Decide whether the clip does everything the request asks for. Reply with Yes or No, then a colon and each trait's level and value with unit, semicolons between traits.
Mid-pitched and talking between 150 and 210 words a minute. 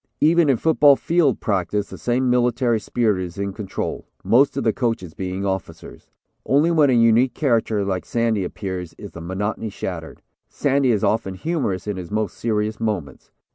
No: low, 110 Hz; average, 175 wpm